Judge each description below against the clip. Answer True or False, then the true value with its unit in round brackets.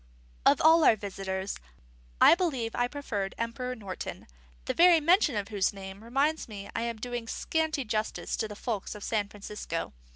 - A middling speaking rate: True (170 wpm)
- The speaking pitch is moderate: False (225 Hz)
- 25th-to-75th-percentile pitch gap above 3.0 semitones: True (5.6 semitones)